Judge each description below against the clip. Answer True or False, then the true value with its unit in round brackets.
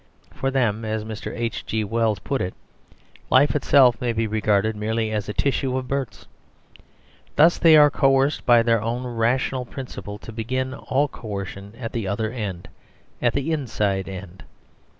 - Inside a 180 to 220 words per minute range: False (160 wpm)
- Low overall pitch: True (115 Hz)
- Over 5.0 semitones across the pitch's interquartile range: False (3.6 semitones)